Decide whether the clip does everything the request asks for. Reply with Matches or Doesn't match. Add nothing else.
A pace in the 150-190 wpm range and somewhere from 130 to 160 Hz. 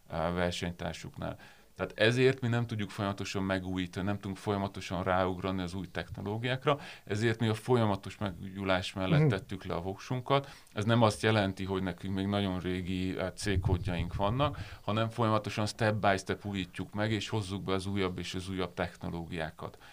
Doesn't match